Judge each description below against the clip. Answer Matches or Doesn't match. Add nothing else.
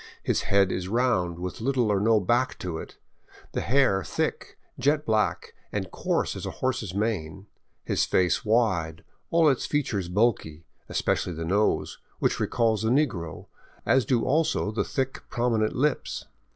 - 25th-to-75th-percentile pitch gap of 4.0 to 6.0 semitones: Matches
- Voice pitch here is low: Matches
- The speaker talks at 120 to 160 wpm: Matches